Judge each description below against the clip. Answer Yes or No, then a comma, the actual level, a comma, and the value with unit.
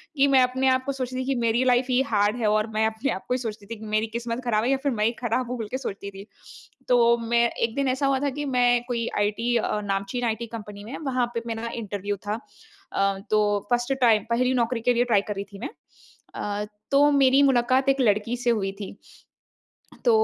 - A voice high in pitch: Yes, high, 235 Hz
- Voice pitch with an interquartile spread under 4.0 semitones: Yes, average, 3.2 semitones